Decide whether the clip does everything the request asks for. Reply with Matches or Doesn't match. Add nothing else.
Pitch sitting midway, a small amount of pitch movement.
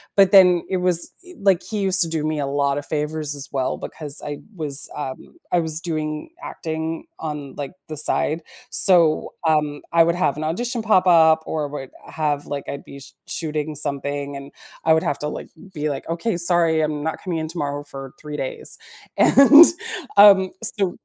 Doesn't match